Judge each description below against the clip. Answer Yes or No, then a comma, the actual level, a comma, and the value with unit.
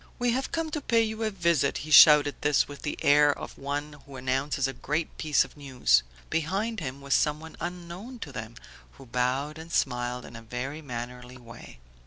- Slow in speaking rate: No, average, 195 wpm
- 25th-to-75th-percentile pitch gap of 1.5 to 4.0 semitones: No, average, 4.7 semitones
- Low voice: No, medium, 145 Hz